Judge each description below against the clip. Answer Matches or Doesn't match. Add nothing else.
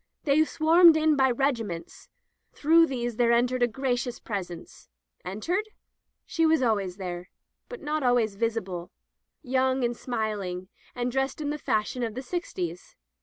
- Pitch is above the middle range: Matches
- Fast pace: Doesn't match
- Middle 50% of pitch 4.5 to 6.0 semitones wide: Matches